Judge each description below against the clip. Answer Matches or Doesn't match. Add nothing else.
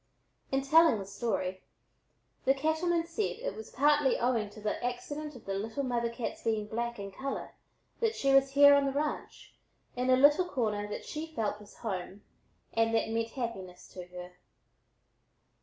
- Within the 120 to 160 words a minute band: Doesn't match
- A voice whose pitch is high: Matches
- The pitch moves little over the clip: Doesn't match